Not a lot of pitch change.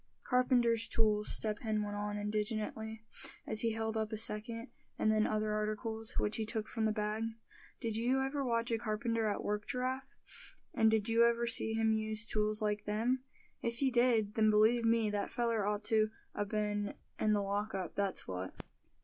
Yes: narrow, 1.6 semitones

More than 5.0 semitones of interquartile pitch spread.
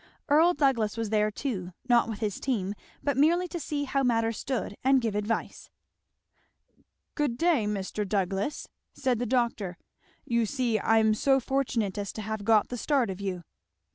No: average, 4.4 semitones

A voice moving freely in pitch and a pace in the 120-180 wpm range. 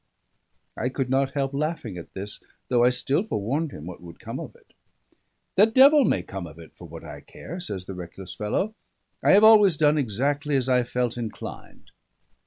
No: wide, 7.5 semitones; average, 195 wpm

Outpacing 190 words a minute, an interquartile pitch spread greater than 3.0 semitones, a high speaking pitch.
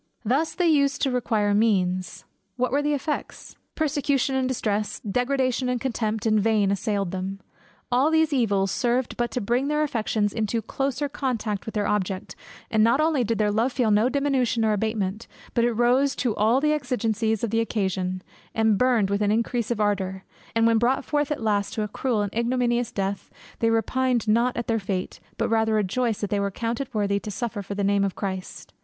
Yes: average, 200 wpm; average, 3.7 semitones; high, 225 Hz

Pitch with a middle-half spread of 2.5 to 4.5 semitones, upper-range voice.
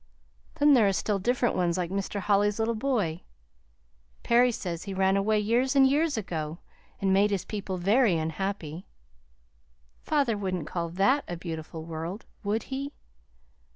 No: average, 4.9 semitones; high, 200 Hz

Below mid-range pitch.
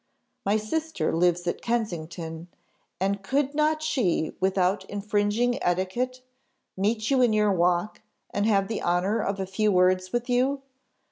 No: high, 205 Hz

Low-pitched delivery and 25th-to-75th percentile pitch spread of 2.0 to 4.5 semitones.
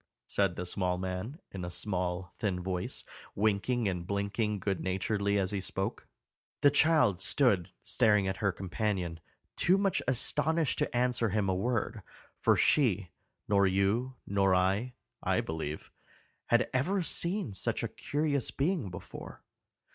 No: low, 100 Hz; average, 5.2 semitones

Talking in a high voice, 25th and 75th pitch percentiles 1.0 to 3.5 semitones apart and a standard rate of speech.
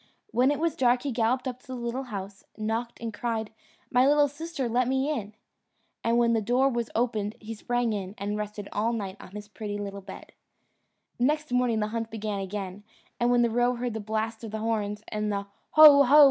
No: high, 230 Hz; average, 2.9 semitones; fast, 215 wpm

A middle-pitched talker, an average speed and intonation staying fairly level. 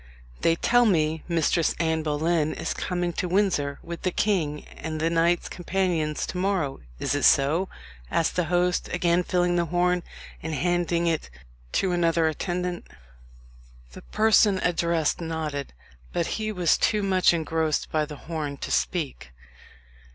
Yes: medium, 170 Hz; average, 150 wpm; narrow, 2.3 semitones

